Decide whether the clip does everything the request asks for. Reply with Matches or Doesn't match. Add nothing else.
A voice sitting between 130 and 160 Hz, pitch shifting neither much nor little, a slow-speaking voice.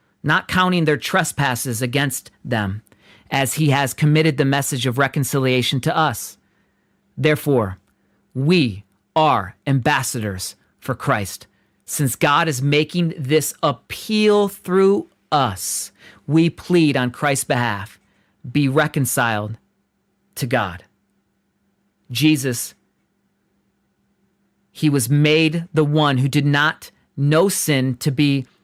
Matches